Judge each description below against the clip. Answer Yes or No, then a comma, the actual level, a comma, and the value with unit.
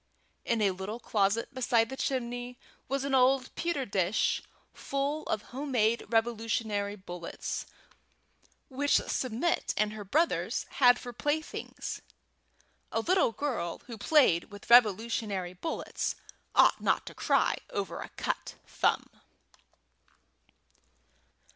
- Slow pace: Yes, slow, 115 wpm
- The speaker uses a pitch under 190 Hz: No, high, 235 Hz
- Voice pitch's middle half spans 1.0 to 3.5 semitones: No, average, 4.4 semitones